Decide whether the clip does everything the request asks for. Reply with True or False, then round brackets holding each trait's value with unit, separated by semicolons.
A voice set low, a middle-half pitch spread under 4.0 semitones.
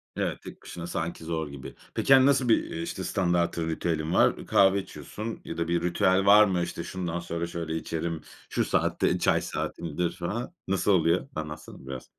True (85 Hz; 2.9 semitones)